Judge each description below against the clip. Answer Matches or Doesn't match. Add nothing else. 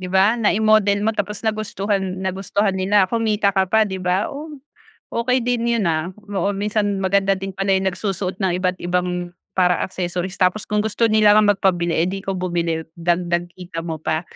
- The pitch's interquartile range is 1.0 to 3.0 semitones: Matches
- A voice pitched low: Doesn't match